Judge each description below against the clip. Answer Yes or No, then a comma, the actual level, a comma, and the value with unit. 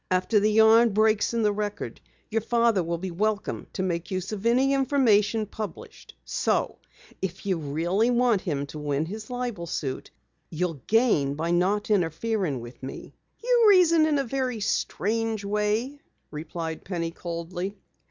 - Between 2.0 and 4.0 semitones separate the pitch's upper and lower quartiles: No, average, 5.1 semitones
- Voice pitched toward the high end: Yes, high, 205 Hz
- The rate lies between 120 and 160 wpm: Yes, average, 155 wpm